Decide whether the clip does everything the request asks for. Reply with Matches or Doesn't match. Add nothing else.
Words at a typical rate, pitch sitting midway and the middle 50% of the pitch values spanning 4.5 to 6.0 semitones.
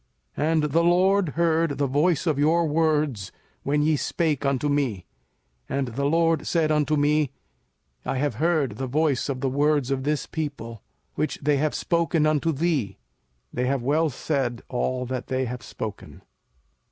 Doesn't match